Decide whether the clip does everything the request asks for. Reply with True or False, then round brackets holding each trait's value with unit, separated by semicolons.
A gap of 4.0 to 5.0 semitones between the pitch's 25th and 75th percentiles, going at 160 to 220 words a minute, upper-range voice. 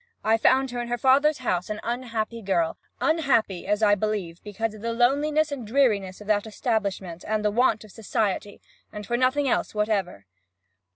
False (3.3 semitones; 180 wpm; 220 Hz)